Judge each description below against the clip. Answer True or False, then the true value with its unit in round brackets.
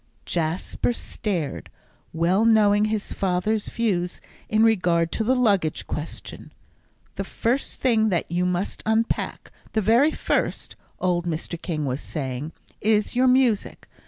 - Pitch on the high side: True (200 Hz)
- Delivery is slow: True (130 wpm)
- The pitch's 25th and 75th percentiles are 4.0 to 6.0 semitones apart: True (4.5 semitones)